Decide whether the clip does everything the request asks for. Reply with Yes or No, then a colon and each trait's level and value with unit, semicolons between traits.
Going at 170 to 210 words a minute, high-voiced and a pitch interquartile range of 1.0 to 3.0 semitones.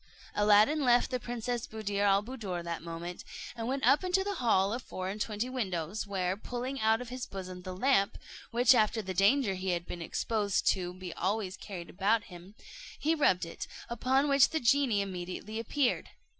No: average, 185 wpm; high, 210 Hz; average, 5.0 semitones